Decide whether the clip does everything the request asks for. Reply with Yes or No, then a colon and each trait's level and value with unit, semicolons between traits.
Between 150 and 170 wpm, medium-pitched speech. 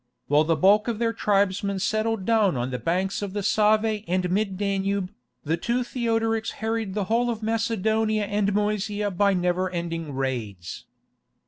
No: average, 160 wpm; high, 205 Hz